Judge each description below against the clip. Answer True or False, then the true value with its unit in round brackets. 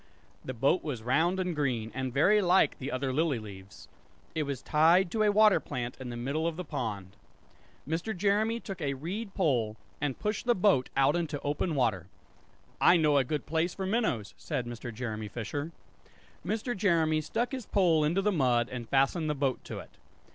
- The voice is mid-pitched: True (150 Hz)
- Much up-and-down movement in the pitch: True (6.5 semitones)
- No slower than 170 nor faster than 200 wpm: True (190 wpm)